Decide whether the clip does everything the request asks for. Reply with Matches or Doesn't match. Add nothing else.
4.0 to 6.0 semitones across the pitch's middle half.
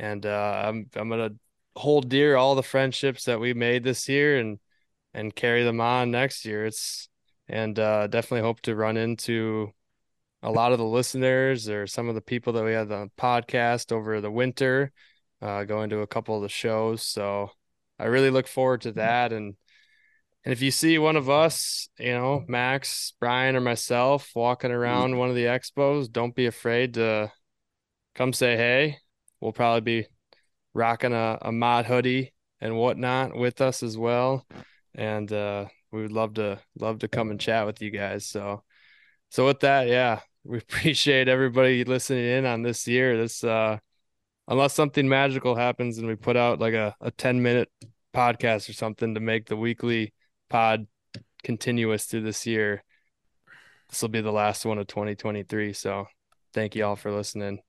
Doesn't match